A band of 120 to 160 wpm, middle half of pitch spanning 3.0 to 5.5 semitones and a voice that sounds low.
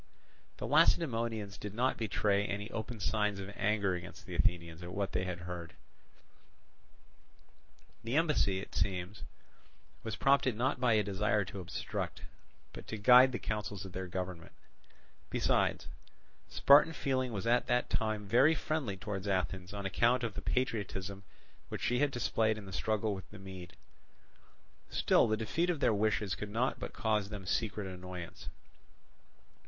Yes: average, 155 wpm; average, 3.5 semitones; low, 105 Hz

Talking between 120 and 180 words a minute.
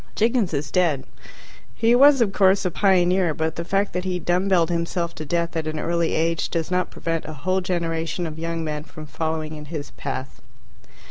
No: average, 200 wpm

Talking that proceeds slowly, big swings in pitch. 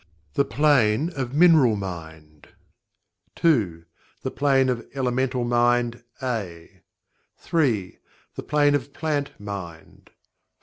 Yes: slow, 105 wpm; wide, 6.1 semitones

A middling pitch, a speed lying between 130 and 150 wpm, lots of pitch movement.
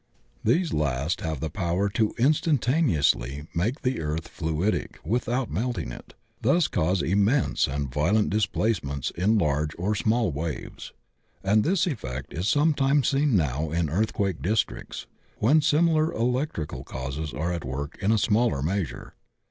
No: very low, 95 Hz; average, 140 wpm; wide, 8.2 semitones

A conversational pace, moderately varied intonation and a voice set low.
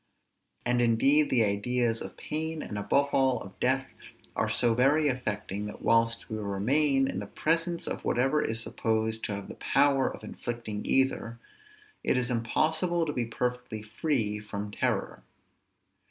Yes: average, 155 wpm; average, 4.0 semitones; low, 120 Hz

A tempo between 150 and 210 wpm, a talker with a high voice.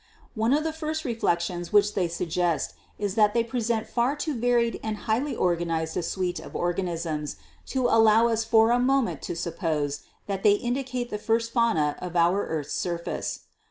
Yes: average, 175 wpm; high, 210 Hz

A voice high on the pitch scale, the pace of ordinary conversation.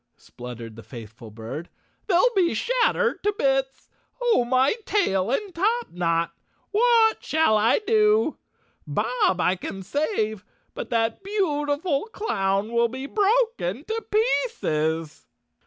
No: very high, 265 Hz; slow, 125 wpm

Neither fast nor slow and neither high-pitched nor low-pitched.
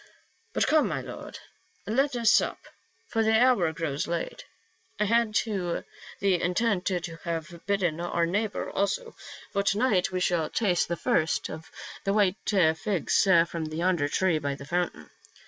Yes: average, 160 wpm; medium, 180 Hz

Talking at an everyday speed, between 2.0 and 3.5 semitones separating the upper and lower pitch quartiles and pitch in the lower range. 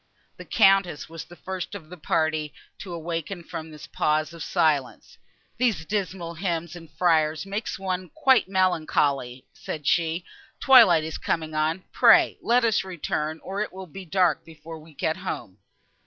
No: average, 160 wpm; average, 3.2 semitones; medium, 170 Hz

